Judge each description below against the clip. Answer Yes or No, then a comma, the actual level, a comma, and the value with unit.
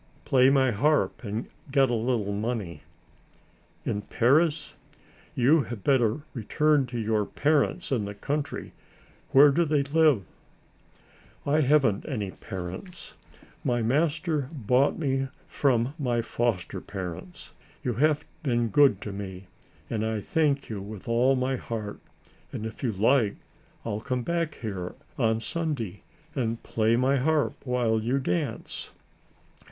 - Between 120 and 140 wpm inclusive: Yes, slow, 135 wpm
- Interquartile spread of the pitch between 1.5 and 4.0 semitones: No, average, 4.7 semitones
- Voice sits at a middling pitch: No, low, 125 Hz